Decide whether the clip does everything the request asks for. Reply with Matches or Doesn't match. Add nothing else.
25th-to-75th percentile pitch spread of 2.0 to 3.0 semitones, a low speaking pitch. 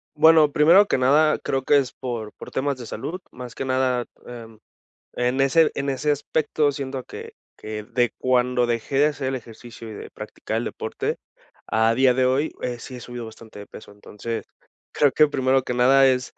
Matches